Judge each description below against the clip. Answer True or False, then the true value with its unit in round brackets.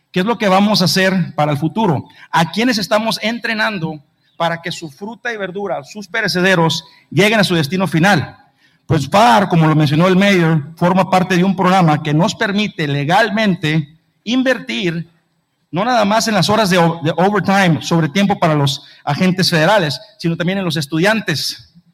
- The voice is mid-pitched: True (180 Hz)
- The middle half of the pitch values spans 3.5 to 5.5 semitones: True (4.2 semitones)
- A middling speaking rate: True (170 wpm)